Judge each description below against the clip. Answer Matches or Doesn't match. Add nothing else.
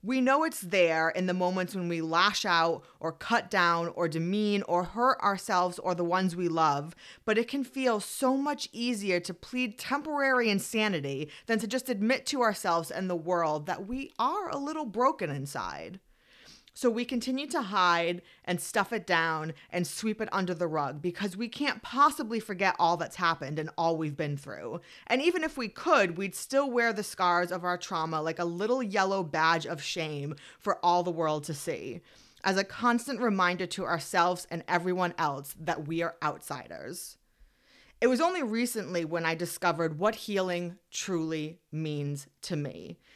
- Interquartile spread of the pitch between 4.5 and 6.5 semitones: Matches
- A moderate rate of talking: Matches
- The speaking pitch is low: Doesn't match